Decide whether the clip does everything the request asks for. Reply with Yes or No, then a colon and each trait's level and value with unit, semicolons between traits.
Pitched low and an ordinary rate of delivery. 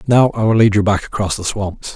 No: low, 105 Hz; fast, 275 wpm